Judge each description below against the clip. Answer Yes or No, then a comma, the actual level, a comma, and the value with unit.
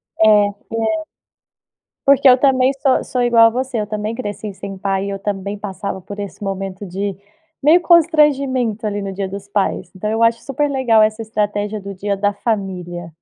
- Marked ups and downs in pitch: No, average, 4.0 semitones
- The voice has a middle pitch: No, high, 210 Hz